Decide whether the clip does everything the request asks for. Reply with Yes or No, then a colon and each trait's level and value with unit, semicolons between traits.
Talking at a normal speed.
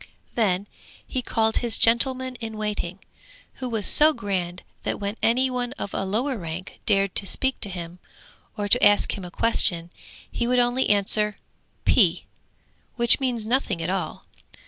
Yes: average, 165 wpm